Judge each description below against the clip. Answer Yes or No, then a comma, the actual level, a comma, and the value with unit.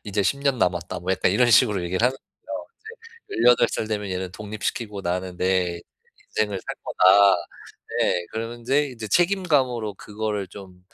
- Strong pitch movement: No, average, 4.3 semitones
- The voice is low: Yes, low, 105 Hz